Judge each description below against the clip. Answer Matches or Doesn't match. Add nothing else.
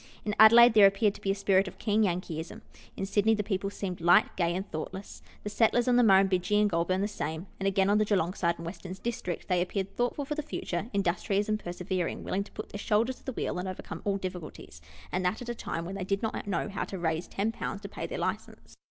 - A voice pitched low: Doesn't match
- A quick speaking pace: Matches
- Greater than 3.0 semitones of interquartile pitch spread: Doesn't match